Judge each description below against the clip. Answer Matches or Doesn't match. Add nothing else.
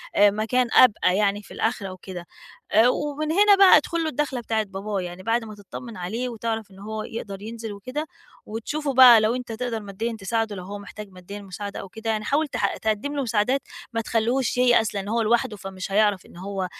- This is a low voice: Doesn't match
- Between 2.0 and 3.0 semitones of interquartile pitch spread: Doesn't match